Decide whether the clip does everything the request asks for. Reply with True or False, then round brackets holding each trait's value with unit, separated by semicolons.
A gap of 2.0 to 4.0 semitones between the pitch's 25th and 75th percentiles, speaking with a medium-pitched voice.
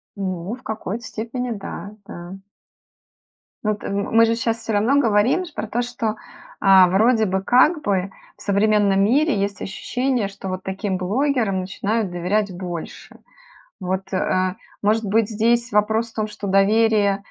False (2.8 semitones; 210 Hz)